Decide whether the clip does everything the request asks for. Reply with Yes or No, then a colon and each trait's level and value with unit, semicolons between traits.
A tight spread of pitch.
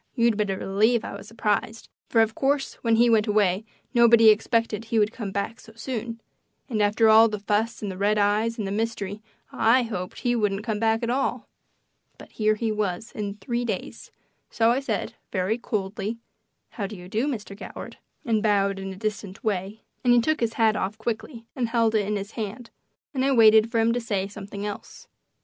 Yes: narrow, 2.1 semitones